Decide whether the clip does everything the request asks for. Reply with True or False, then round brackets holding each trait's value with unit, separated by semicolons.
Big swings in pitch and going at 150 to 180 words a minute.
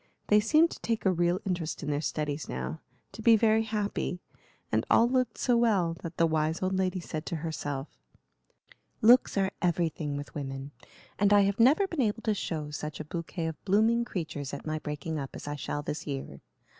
False (6.0 semitones; 200 wpm)